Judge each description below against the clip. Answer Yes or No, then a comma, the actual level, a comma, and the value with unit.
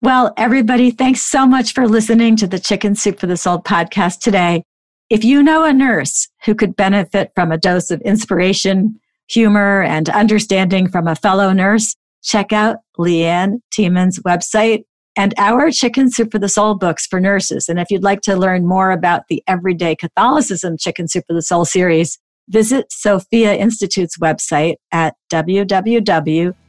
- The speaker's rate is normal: Yes, average, 165 wpm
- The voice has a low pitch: No, high, 195 Hz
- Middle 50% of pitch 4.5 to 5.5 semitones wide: No, average, 3.6 semitones